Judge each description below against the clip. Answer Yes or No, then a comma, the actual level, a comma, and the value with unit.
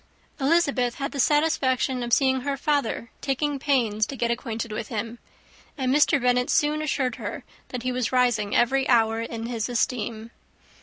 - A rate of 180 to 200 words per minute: No, average, 165 wpm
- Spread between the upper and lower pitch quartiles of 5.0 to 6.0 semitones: No, average, 3.0 semitones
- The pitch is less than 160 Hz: No, very high, 250 Hz